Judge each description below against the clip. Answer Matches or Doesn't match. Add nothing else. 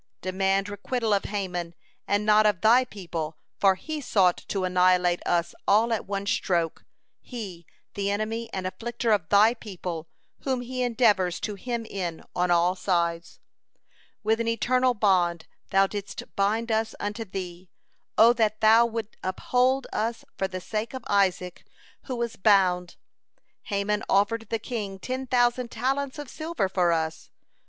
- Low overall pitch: Doesn't match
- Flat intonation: Doesn't match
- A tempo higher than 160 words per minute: Doesn't match